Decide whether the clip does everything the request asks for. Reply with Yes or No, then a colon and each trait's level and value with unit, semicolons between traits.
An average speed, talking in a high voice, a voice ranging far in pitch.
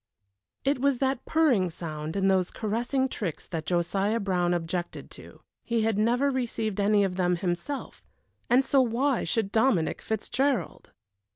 Yes: average, 150 wpm; high, 215 Hz; wide, 6.1 semitones